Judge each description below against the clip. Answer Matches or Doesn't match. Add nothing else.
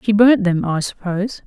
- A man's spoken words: Doesn't match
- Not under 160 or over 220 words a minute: Matches